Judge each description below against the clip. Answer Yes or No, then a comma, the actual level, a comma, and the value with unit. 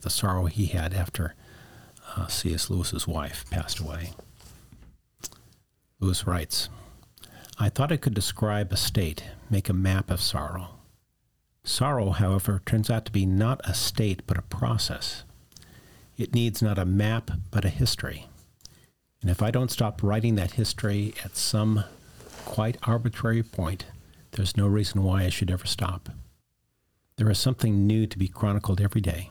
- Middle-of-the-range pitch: No, low, 100 Hz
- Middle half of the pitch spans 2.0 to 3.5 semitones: Yes, average, 2.9 semitones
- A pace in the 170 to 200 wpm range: No, average, 155 wpm